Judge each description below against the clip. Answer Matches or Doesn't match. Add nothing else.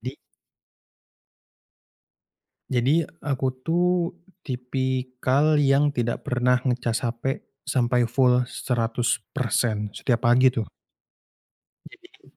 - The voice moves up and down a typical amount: Doesn't match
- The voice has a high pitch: Doesn't match